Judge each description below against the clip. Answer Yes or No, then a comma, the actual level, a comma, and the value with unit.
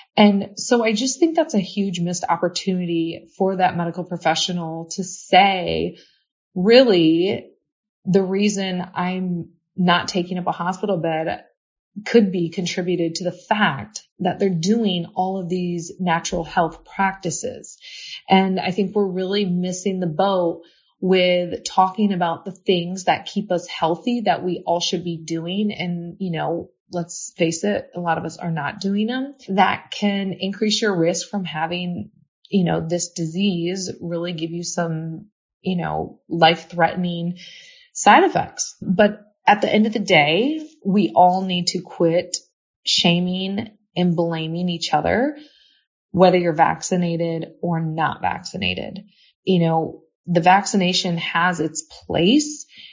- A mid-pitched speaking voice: Yes, medium, 180 Hz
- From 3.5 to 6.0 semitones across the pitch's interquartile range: No, average, 2.8 semitones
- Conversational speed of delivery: Yes, average, 145 wpm